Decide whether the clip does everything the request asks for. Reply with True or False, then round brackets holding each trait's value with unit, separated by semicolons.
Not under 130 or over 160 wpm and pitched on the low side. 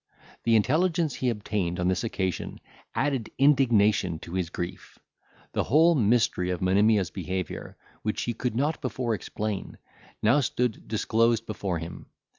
True (140 wpm; 110 Hz)